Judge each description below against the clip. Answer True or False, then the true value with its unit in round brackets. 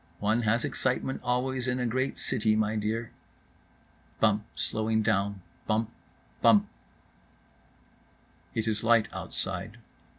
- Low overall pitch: True (110 Hz)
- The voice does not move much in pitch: True (2.0 semitones)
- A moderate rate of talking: False (105 wpm)